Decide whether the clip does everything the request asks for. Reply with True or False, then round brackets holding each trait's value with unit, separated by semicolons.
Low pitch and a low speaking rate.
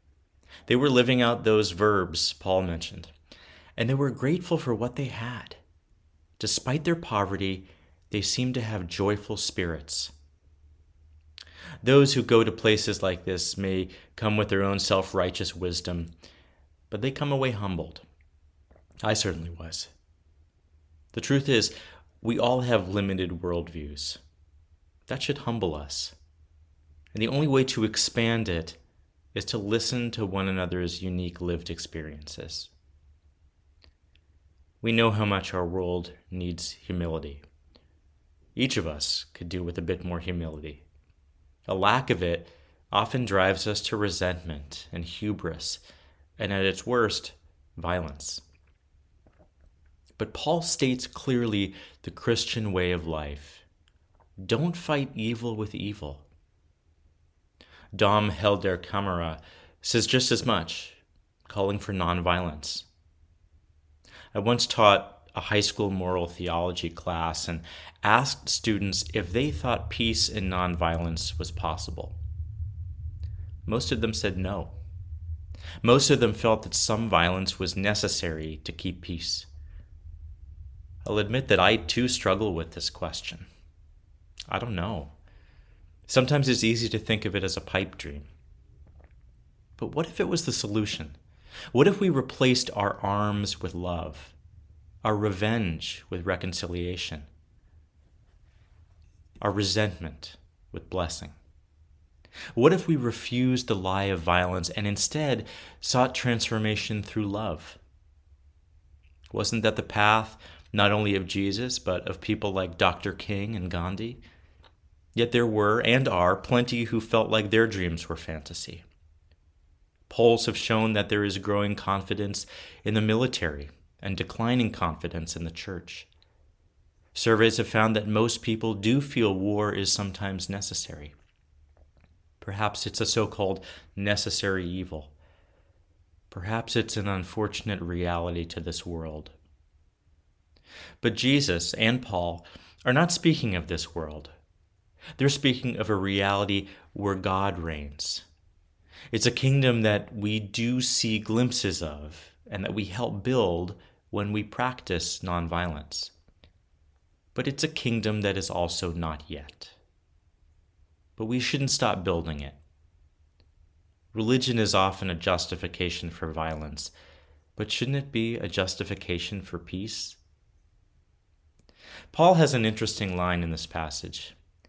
True (90 Hz; 130 wpm)